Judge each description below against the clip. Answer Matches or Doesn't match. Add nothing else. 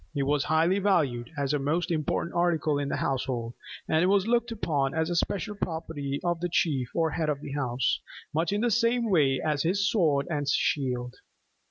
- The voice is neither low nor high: Matches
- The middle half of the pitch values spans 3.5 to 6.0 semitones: Matches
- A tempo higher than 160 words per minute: Matches